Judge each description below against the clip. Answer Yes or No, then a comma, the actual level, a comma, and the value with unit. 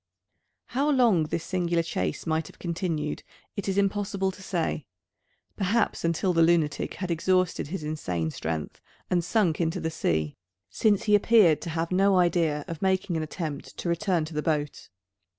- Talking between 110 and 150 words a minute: No, average, 170 wpm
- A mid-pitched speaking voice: Yes, medium, 170 Hz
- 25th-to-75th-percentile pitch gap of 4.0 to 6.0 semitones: No, average, 3.4 semitones